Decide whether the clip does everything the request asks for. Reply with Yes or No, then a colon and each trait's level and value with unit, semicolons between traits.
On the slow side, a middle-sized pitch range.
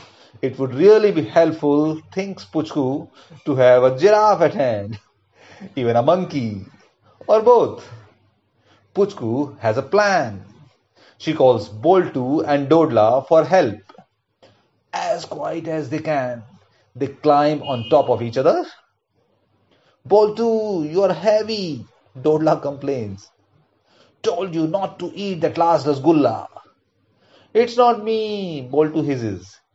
No: slow, 120 wpm; wide, 6.8 semitones